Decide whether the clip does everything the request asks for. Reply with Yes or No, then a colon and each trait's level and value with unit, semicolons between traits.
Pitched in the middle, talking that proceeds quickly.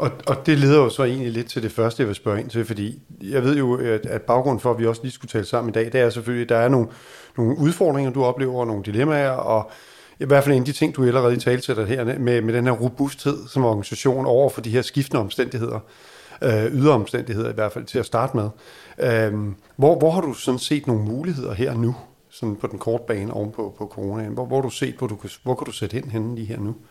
No: low, 120 Hz; fast, 250 wpm